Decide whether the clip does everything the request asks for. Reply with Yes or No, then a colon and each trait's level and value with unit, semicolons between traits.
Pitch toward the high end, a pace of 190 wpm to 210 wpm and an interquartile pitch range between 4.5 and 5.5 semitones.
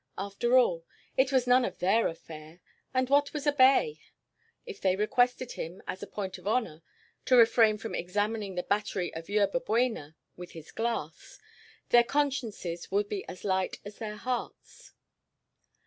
No: high, 210 Hz; average, 165 wpm; average, 5.2 semitones